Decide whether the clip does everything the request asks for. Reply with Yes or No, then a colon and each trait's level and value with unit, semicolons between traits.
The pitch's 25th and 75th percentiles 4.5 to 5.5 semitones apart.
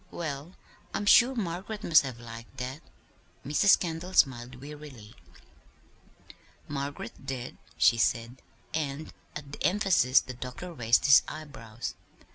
Yes: average, 5.1 semitones